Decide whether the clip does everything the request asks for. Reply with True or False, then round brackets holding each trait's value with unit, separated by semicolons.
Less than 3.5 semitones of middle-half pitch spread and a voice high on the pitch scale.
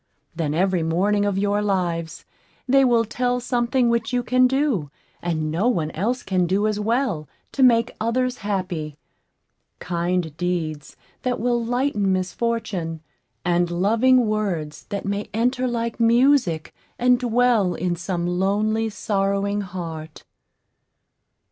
False (5.3 semitones; 205 Hz)